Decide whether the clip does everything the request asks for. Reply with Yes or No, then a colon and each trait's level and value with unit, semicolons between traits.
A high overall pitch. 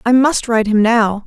Yes: high, 230 Hz